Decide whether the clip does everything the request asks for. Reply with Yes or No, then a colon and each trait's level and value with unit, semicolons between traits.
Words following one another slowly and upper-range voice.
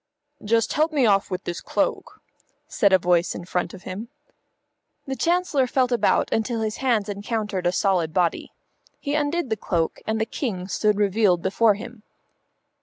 No: average, 170 wpm; high, 210 Hz